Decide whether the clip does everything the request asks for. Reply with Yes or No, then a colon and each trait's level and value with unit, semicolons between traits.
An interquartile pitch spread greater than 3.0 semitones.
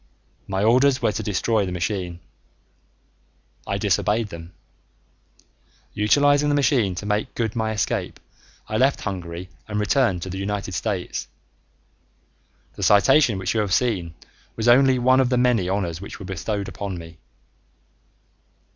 Yes: average, 4.5 semitones